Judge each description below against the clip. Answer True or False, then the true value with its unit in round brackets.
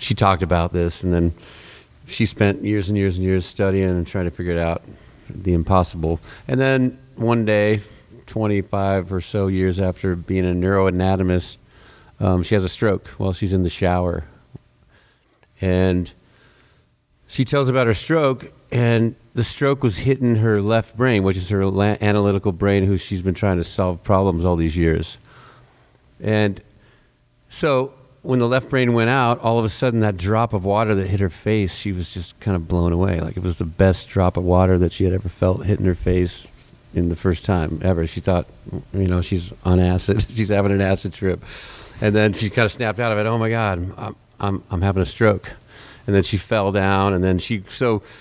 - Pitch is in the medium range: False (100 Hz)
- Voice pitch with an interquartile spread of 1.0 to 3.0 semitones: False (3.6 semitones)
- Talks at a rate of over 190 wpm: True (200 wpm)